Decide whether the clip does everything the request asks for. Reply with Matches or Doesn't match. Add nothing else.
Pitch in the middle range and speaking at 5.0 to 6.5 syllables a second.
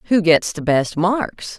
Doesn't match